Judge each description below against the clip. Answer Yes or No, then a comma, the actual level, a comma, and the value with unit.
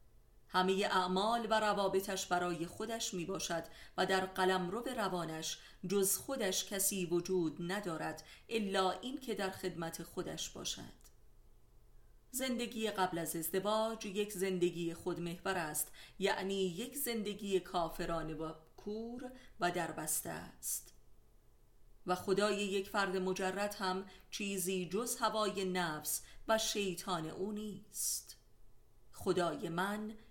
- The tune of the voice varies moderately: Yes, average, 3.1 semitones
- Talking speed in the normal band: Yes, average, 115 wpm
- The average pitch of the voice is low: No, high, 190 Hz